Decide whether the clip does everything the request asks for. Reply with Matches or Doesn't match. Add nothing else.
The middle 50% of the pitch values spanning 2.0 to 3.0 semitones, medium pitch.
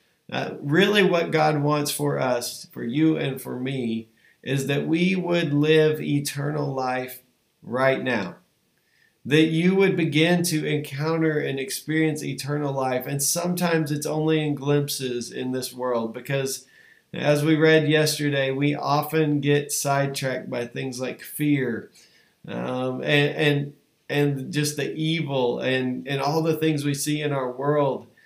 Matches